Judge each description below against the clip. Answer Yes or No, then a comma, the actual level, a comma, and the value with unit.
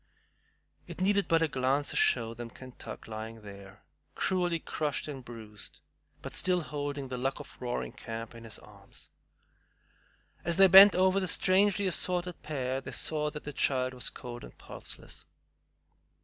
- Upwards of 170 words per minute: No, average, 160 wpm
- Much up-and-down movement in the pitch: Yes, wide, 6.8 semitones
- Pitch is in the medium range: Yes, medium, 145 Hz